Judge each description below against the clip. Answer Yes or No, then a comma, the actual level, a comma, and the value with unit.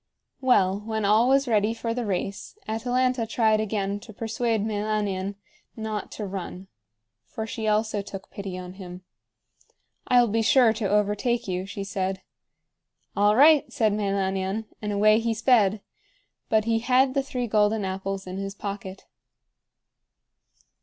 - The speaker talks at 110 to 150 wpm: Yes, average, 145 wpm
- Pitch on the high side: Yes, high, 210 Hz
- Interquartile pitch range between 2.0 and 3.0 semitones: Yes, narrow, 2.4 semitones